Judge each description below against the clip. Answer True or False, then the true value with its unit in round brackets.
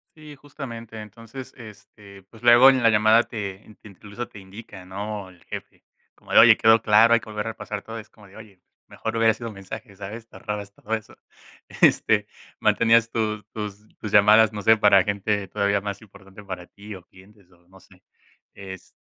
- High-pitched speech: False (105 Hz)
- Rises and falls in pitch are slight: True (2.1 semitones)